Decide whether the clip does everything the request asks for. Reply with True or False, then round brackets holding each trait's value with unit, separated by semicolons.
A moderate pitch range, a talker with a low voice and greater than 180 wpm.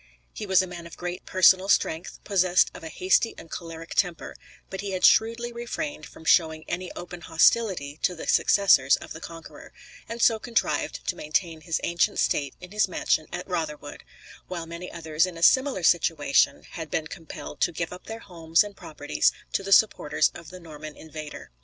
False (3.0 semitones; 175 Hz; 190 wpm)